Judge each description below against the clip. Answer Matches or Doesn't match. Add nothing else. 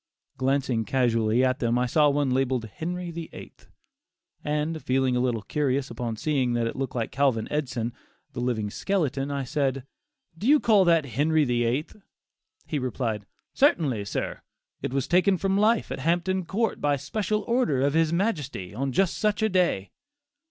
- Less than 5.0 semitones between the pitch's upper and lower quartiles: Doesn't match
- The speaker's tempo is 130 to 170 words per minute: Matches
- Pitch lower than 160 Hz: Matches